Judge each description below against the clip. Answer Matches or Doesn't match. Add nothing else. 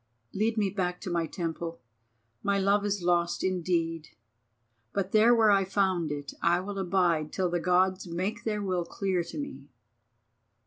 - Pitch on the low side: Doesn't match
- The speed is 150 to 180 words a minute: Matches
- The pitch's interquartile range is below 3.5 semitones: Matches